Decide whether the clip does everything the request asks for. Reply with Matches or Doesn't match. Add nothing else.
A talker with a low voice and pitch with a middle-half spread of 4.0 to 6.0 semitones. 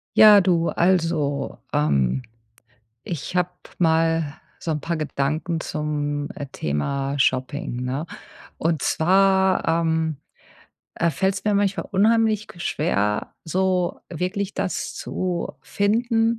Doesn't match